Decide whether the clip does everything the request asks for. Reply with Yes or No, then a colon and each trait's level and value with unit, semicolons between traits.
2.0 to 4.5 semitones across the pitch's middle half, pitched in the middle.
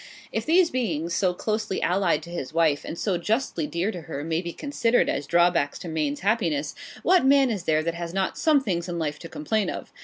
No: wide, 5.4 semitones; medium, 175 Hz